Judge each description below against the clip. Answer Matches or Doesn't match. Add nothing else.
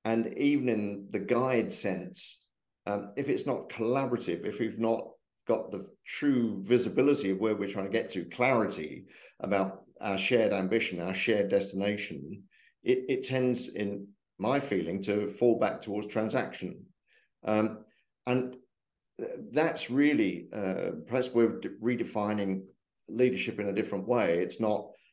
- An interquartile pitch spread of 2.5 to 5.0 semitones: Matches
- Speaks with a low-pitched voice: Matches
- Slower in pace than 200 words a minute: Matches